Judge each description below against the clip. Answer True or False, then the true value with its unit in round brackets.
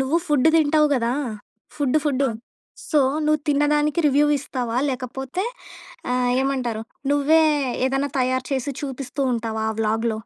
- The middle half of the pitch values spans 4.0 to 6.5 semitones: False (2.9 semitones)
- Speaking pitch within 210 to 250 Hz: False (270 Hz)